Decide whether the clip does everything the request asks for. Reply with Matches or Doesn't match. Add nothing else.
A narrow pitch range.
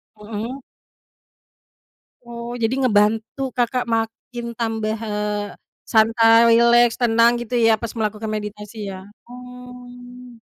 Matches